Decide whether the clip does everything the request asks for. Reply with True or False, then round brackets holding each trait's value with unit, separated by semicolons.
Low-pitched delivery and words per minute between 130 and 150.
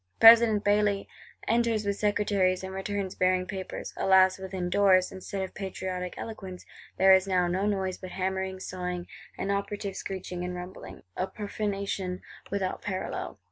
False (190 Hz; 145 wpm)